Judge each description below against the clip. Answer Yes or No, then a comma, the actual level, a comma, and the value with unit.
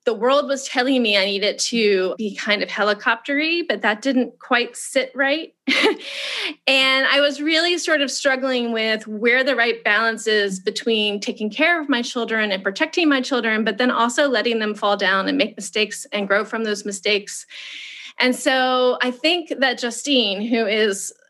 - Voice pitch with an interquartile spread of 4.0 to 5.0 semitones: Yes, average, 4.4 semitones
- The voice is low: No, high, 245 Hz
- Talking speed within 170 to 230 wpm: Yes, average, 180 wpm